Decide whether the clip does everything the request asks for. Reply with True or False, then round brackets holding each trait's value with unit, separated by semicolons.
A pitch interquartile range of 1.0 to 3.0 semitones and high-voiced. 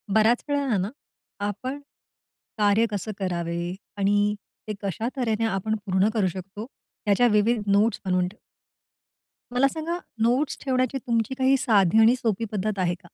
False (3.7 semitones; 215 Hz)